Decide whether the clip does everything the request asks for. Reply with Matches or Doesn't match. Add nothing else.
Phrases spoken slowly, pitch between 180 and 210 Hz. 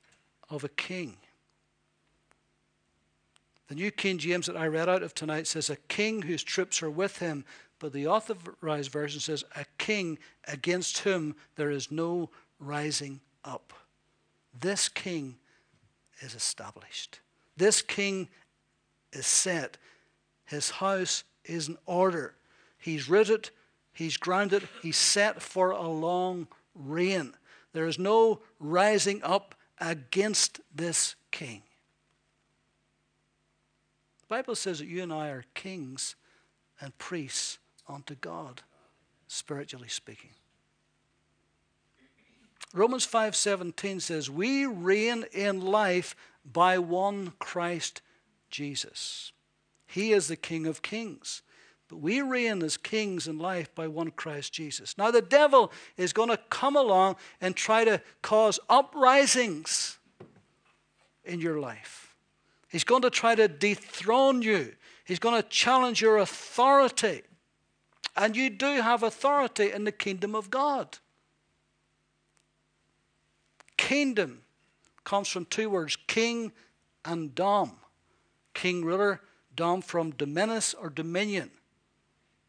Matches